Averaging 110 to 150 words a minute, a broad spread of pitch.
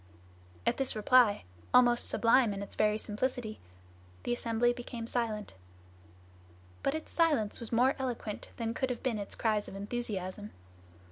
No: average, 145 wpm; average, 2.8 semitones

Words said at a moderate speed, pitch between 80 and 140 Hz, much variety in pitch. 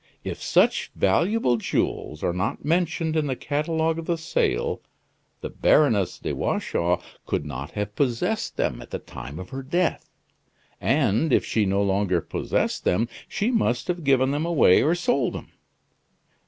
Yes: average, 160 wpm; low, 135 Hz; wide, 8.6 semitones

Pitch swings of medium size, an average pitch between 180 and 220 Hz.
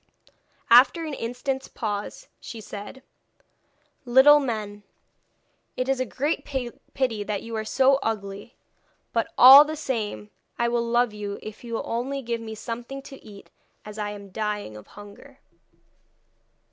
No: average, 4.0 semitones; high, 235 Hz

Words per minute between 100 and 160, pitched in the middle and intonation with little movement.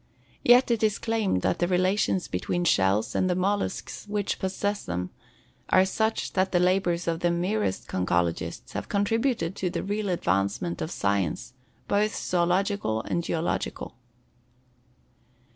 No: average, 140 wpm; medium, 180 Hz; average, 4.2 semitones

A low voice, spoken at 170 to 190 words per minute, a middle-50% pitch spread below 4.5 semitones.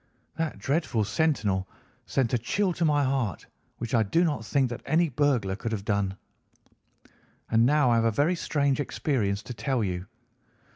No: low, 125 Hz; average, 175 wpm; wide, 5.5 semitones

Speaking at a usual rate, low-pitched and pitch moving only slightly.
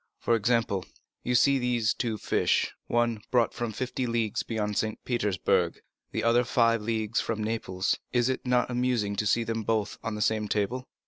Yes: average, 180 wpm; low, 115 Hz; narrow, 2.3 semitones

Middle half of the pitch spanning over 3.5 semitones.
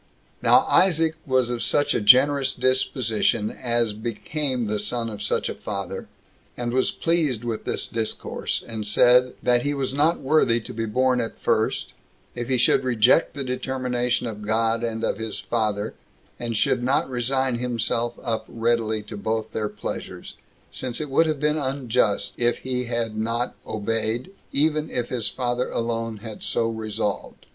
No: narrow, 2.5 semitones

